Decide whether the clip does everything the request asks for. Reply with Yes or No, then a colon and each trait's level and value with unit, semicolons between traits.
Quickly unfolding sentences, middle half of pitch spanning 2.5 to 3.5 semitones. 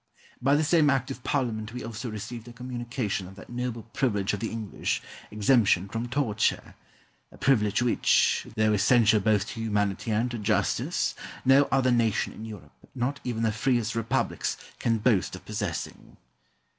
No: average, 165 wpm; average, 2.8 semitones